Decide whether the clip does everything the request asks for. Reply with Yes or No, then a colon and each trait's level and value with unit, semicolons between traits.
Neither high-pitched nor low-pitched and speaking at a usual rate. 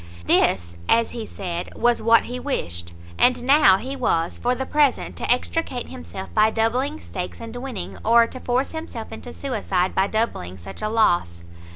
No: high, 230 Hz; average, 175 wpm